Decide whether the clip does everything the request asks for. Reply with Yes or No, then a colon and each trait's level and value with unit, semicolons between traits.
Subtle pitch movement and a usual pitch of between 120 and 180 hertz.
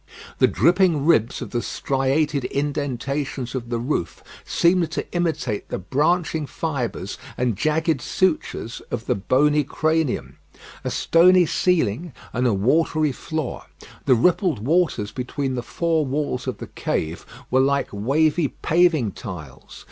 No: average, 4.8 semitones; medium, 140 Hz